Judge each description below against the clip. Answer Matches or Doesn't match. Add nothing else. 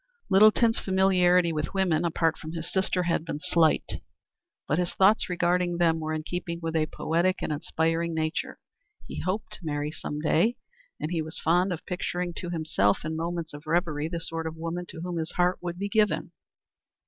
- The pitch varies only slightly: Matches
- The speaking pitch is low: Doesn't match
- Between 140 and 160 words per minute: Doesn't match